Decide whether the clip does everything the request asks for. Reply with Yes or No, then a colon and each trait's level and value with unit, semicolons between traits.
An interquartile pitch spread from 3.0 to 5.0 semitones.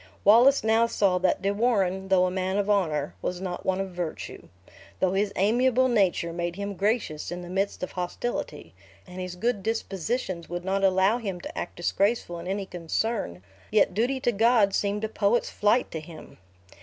Yes: average, 3.5 semitones